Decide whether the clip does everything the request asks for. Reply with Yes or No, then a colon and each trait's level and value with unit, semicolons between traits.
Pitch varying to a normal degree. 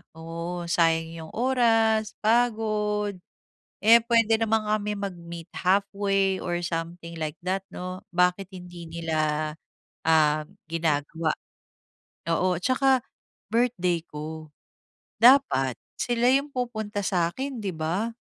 Yes: average, 5.0 semitones